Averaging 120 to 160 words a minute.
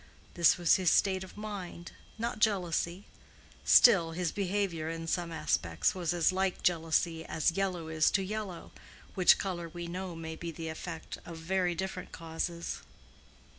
Yes: average, 150 wpm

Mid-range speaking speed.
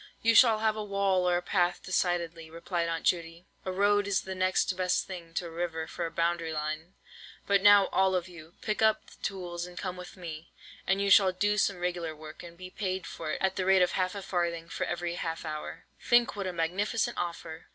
No: fast, 225 wpm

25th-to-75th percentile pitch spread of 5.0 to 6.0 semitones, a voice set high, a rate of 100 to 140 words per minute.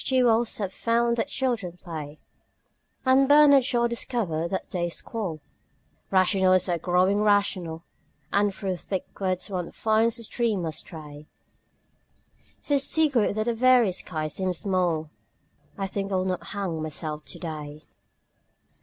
Yes: average, 5.3 semitones; high, 195 Hz; slow, 135 wpm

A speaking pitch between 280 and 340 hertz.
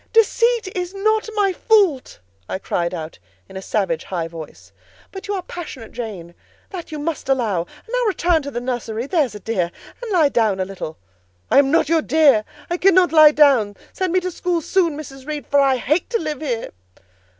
Yes: very high, 295 Hz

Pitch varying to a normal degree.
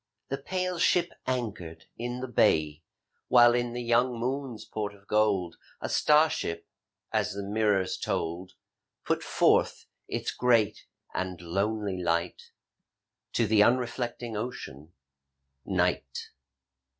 Yes: average, 4.7 semitones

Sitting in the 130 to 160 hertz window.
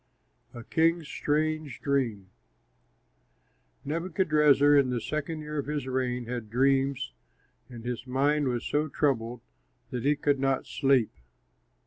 Yes: medium, 140 Hz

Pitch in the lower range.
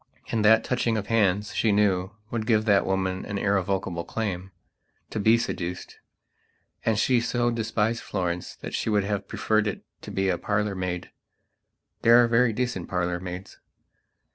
Yes: low, 105 Hz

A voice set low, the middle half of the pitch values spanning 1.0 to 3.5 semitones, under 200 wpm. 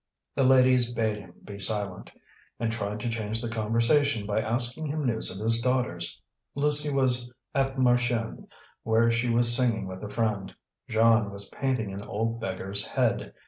Yes: low, 115 Hz; average, 2.9 semitones; average, 165 wpm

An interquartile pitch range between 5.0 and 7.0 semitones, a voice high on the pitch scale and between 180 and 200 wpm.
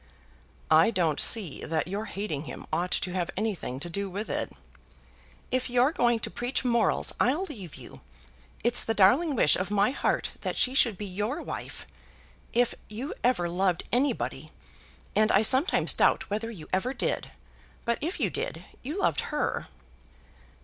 No: average, 5.3 semitones; high, 215 Hz; average, 165 wpm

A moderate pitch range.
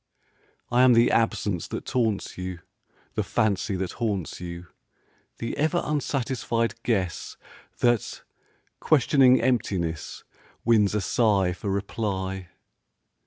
Yes: average, 4.3 semitones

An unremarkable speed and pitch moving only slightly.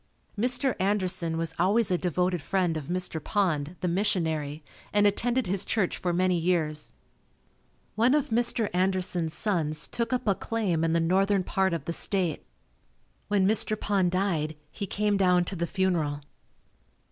No: average, 160 wpm; average, 3.4 semitones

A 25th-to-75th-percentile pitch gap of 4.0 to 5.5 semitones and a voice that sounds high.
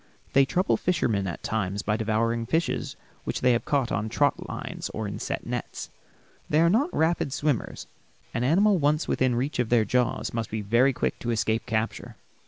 No: average, 5.0 semitones; low, 120 Hz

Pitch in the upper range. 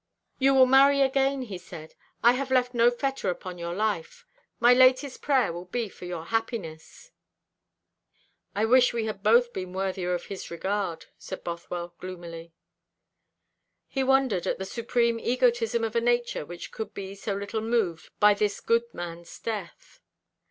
Yes: high, 220 Hz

